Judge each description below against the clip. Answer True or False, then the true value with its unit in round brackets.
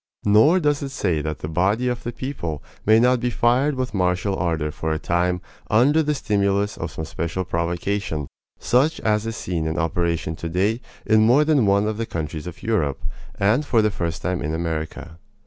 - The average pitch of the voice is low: True (100 Hz)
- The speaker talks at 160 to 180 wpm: False (190 wpm)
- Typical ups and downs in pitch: False (6.1 semitones)